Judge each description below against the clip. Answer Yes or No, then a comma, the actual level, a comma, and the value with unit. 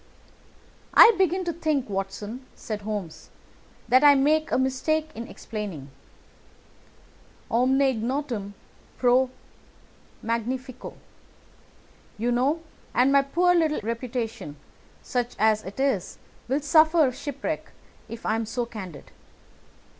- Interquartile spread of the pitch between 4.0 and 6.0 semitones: Yes, average, 4.7 semitones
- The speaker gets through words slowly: Yes, slow, 110 wpm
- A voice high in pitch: Yes, very high, 250 Hz